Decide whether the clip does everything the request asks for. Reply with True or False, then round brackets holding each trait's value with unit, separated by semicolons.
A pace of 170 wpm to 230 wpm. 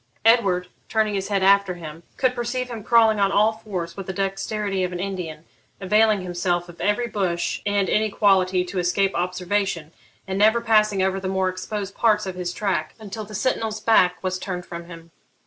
True (185 wpm)